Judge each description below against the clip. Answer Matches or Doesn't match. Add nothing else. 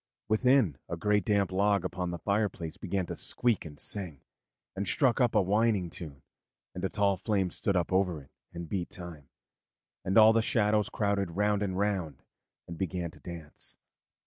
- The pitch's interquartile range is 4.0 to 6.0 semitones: Doesn't match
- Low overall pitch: Matches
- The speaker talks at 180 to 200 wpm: Doesn't match